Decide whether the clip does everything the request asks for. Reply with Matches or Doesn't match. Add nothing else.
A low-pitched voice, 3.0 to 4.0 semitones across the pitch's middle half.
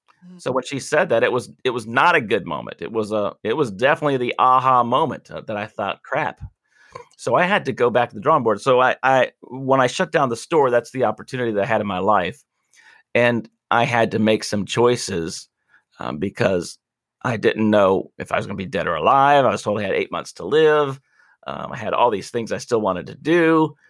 Doesn't match